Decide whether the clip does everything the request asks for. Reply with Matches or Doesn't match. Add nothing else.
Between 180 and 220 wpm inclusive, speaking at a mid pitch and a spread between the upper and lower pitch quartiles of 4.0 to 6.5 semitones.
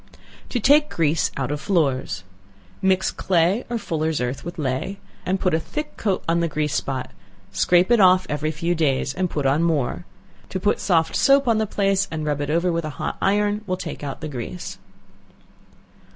Matches